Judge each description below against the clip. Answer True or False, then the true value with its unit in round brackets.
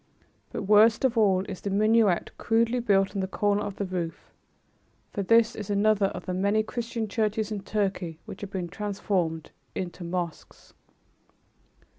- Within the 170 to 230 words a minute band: False (160 wpm)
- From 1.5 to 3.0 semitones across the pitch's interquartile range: True (2.5 semitones)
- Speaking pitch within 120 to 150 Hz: False (205 Hz)